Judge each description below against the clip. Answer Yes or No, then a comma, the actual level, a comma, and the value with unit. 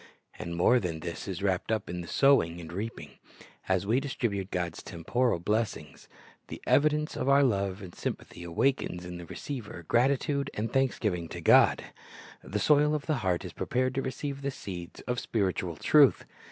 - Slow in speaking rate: No, average, 180 wpm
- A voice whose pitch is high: No, low, 105 Hz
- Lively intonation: Yes, wide, 7.3 semitones